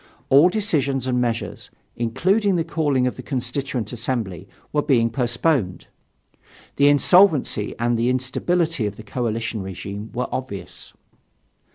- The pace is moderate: No, slow, 130 wpm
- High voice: No, low, 125 Hz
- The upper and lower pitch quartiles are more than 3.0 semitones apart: Yes, average, 4.2 semitones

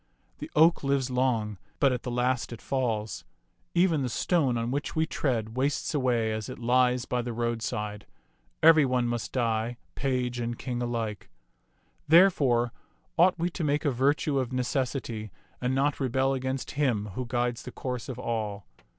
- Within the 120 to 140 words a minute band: No, average, 165 wpm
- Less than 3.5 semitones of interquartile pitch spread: Yes, average, 2.7 semitones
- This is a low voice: Yes, low, 125 Hz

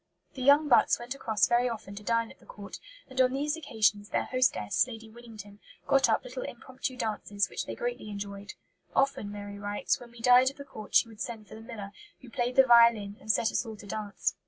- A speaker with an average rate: No, fast, 225 wpm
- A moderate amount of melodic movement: Yes, average, 3.7 semitones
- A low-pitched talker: No, high, 230 Hz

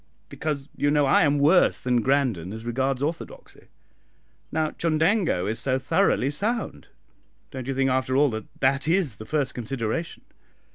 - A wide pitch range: No, average, 3.7 semitones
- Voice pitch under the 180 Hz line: Yes, low, 135 Hz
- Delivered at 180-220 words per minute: No, average, 155 wpm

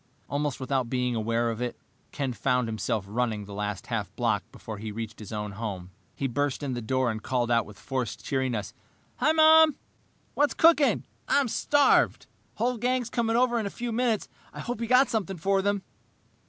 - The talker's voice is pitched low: Yes, low, 130 Hz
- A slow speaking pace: No, average, 195 wpm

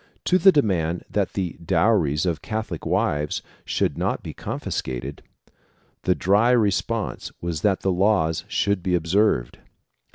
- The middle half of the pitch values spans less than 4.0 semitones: No, average, 4.7 semitones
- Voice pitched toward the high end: No, very low, 95 Hz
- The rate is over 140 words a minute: No, slow, 135 wpm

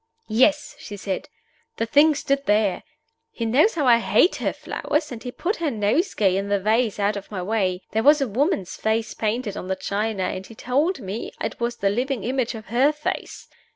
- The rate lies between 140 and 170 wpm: No, fast, 205 wpm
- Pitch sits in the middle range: No, high, 225 Hz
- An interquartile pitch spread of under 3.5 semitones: No, wide, 5.4 semitones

